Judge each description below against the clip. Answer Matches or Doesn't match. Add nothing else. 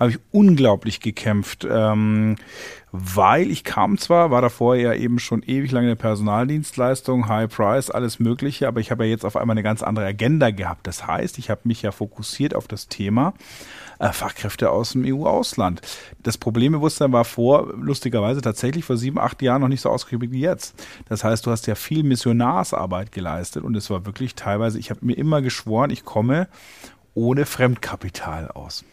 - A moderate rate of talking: Matches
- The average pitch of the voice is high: Doesn't match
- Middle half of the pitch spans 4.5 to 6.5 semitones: Doesn't match